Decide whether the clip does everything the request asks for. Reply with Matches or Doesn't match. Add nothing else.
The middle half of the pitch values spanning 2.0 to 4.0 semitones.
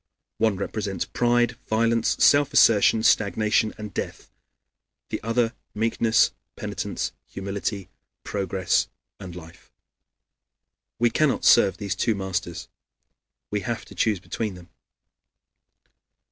Matches